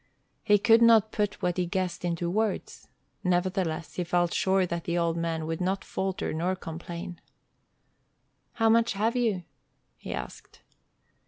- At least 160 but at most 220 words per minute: No, average, 150 wpm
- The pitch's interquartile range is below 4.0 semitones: Yes, average, 3.3 semitones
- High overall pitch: No, medium, 180 Hz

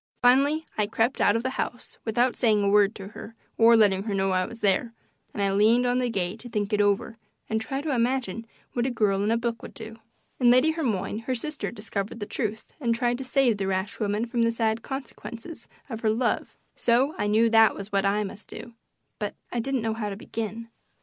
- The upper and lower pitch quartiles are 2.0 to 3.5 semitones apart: Yes, average, 2.8 semitones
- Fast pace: Yes, fast, 230 wpm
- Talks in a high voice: Yes, high, 225 Hz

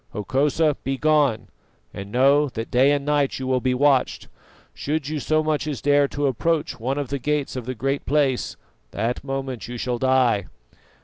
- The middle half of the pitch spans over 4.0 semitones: No, narrow, 2.5 semitones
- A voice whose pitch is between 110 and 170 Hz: Yes, low, 135 Hz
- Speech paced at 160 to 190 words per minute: Yes, average, 180 wpm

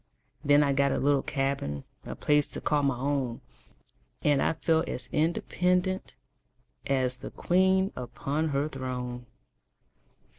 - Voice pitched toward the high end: No, medium, 140 Hz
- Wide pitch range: No, average, 3.5 semitones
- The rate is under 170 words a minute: Yes, slow, 135 wpm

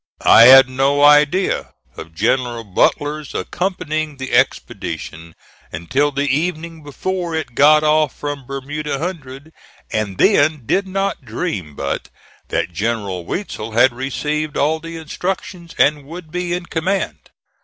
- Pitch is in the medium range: Yes, medium, 145 Hz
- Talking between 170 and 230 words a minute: No, slow, 135 wpm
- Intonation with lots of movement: No, average, 4.8 semitones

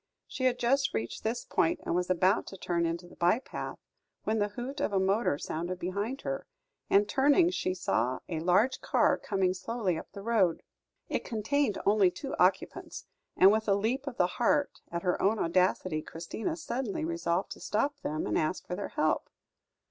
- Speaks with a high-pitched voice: Yes, high, 195 Hz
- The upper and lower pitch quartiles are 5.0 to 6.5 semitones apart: Yes, average, 5.3 semitones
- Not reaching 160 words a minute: No, average, 190 wpm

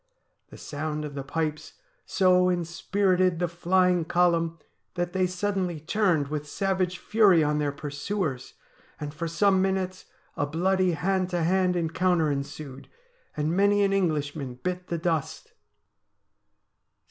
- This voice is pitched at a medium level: Yes, medium, 175 Hz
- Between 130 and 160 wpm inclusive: Yes, slow, 135 wpm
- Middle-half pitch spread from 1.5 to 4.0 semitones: Yes, average, 3.4 semitones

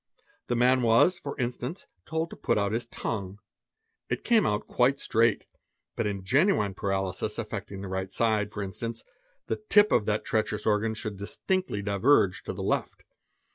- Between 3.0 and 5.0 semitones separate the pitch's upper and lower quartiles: Yes, average, 3.9 semitones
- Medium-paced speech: Yes, average, 175 wpm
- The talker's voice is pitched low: Yes, low, 110 Hz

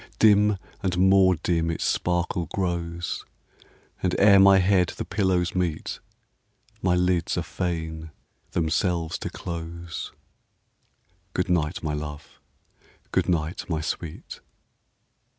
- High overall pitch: No, very low, 90 Hz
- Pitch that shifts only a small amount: Yes, narrow, 2.0 semitones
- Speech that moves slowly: Yes, slow, 115 wpm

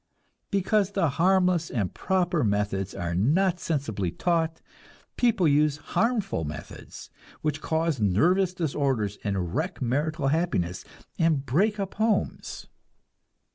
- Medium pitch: Yes, medium, 155 Hz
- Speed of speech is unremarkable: No, slow, 115 wpm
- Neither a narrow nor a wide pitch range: No, wide, 8.4 semitones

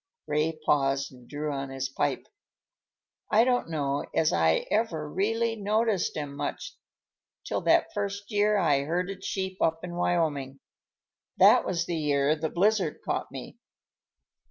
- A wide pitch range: Yes, wide, 6.0 semitones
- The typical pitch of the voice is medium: Yes, medium, 165 Hz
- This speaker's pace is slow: No, average, 145 wpm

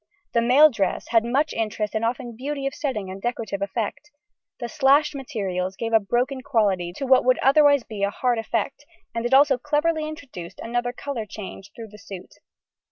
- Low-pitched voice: No, high, 240 Hz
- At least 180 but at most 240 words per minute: Yes, average, 185 wpm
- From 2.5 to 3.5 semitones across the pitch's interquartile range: No, average, 4.5 semitones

